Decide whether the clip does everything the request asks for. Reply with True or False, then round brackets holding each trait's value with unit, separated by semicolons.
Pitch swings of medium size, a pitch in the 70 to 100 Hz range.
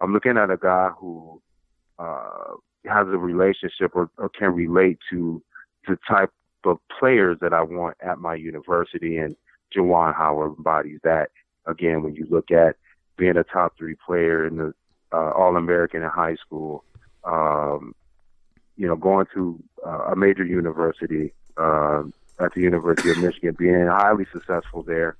False (2.0 semitones; 85 Hz)